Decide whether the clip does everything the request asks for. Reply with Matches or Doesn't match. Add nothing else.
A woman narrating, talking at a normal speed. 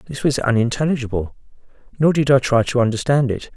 Doesn't match